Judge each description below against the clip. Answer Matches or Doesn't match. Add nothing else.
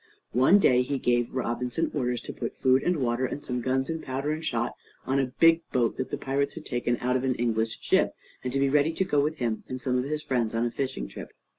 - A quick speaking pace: Matches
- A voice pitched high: Doesn't match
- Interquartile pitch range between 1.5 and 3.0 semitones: Matches